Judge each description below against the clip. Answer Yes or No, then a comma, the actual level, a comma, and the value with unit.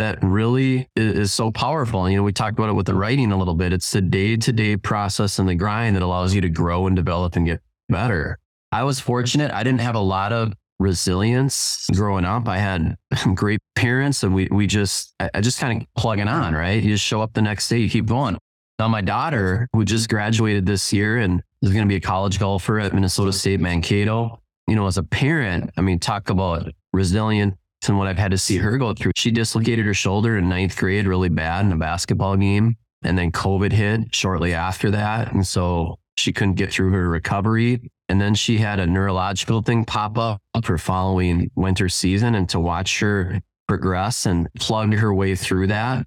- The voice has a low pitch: Yes, low, 100 Hz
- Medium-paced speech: No, fast, 215 wpm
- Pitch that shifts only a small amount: No, average, 3.2 semitones